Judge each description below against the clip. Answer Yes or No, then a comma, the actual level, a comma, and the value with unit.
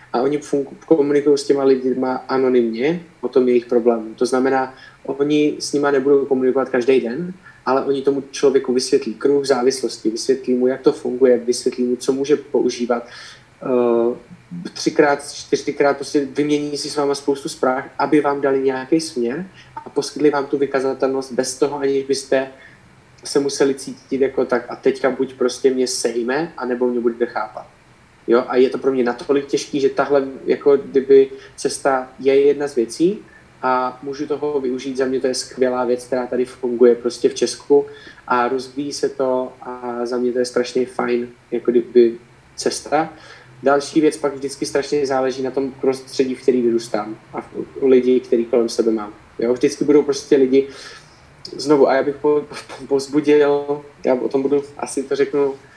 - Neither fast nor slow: No, fast, 170 wpm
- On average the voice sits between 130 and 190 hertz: Yes, low, 135 Hz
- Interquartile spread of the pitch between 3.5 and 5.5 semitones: No, narrow, 2.4 semitones